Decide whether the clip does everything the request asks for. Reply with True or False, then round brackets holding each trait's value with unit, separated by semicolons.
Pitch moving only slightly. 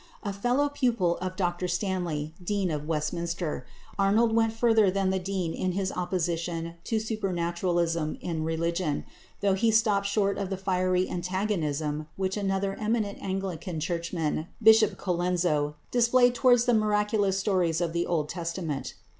False (3.5 semitones)